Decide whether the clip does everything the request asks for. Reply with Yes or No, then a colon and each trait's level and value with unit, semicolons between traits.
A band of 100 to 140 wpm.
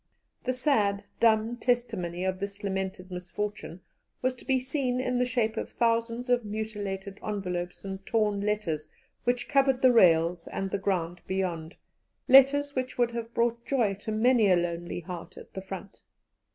No: average, 165 wpm